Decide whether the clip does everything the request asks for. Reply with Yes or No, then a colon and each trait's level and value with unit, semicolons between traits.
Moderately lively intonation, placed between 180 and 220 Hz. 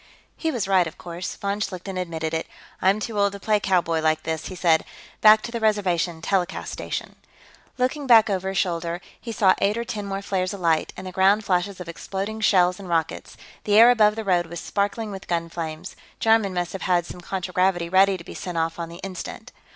Yes: average, 3.0 semitones; high, 190 Hz